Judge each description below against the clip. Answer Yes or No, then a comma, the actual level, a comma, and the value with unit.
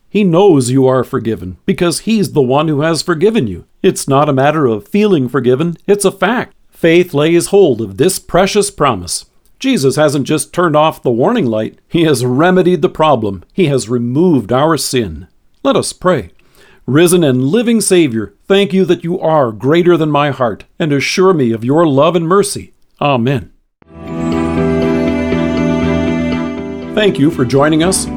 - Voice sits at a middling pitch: Yes, medium, 150 Hz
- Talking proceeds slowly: No, average, 165 wpm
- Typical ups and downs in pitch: No, wide, 6.9 semitones